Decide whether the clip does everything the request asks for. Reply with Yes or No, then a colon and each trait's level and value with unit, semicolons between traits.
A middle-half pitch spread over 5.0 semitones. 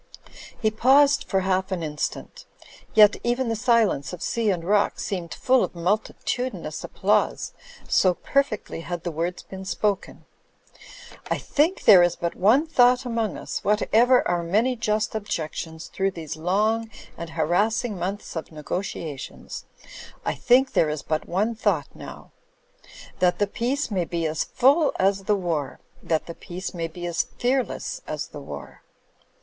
Yes: wide, 5.4 semitones